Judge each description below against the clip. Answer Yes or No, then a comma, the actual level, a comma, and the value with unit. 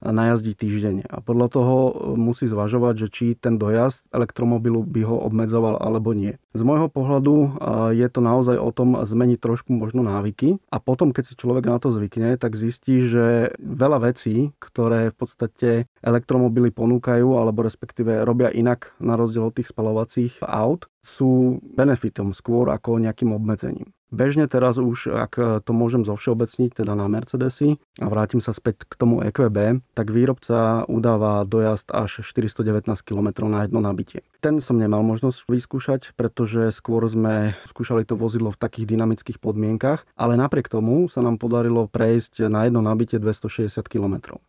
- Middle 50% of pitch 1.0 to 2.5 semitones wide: Yes, narrow, 1.8 semitones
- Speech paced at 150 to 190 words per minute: Yes, average, 160 wpm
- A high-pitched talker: No, low, 115 Hz